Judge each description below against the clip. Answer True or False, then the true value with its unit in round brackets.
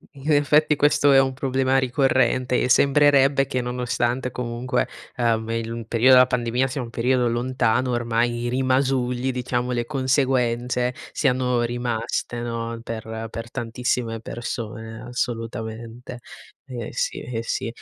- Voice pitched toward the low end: True (125 Hz)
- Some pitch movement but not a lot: False (1.8 semitones)